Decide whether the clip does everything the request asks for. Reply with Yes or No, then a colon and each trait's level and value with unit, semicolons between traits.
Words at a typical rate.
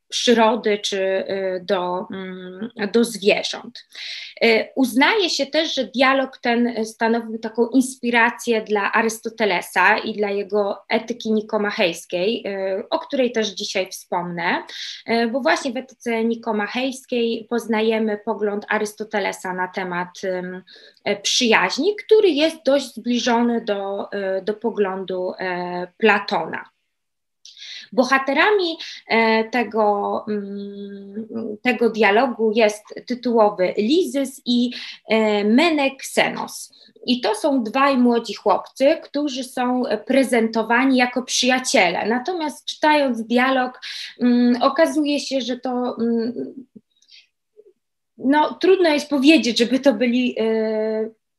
No: slow, 90 wpm